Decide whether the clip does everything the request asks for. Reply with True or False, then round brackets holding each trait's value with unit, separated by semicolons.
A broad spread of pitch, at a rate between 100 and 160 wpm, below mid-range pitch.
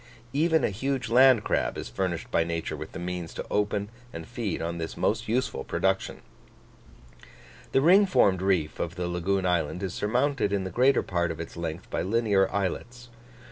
False (5.7 semitones; 180 wpm; 95 Hz)